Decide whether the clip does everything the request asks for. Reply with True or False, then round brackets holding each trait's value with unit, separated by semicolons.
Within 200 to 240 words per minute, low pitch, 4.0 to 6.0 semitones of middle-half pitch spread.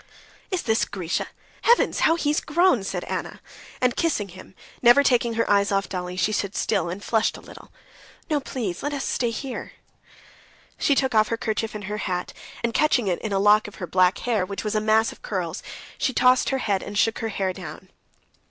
False (205 wpm; 215 Hz; 4.4 semitones)